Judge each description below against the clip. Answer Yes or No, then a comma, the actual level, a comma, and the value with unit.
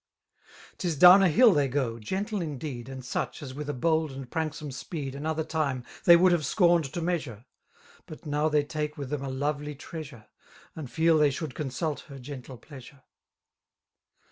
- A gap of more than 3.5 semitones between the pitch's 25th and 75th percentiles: No, average, 3.1 semitones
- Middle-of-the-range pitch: Yes, medium, 150 Hz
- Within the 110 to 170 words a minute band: No, average, 180 wpm